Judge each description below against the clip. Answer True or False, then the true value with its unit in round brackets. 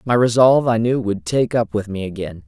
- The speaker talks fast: True (240 wpm)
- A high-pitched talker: False (110 Hz)